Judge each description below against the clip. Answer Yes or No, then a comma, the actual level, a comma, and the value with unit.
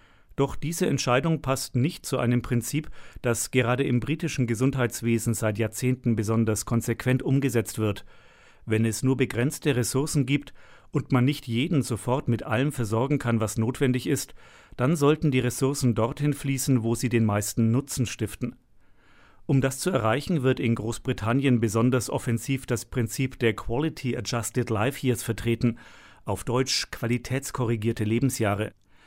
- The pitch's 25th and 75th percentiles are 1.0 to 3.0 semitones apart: Yes, average, 2.7 semitones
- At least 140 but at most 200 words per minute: Yes, average, 145 wpm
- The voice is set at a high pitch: No, low, 125 Hz